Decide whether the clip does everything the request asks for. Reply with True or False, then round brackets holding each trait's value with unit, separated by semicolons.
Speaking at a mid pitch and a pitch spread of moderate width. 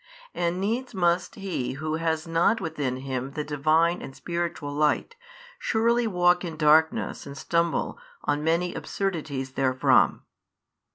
True (160 Hz; 3.3 semitones)